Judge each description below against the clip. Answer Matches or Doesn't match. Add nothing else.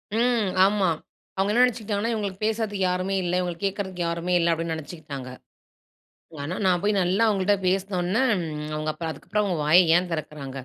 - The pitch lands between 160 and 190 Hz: Matches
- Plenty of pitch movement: Doesn't match